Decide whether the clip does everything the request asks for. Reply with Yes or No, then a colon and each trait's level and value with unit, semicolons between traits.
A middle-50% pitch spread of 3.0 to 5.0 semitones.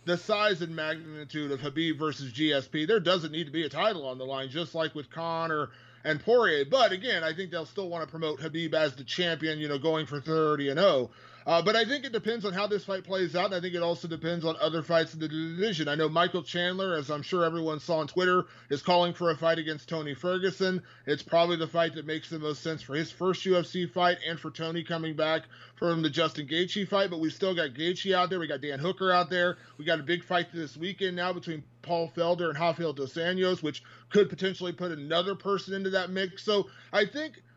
No: narrow, 2.6 semitones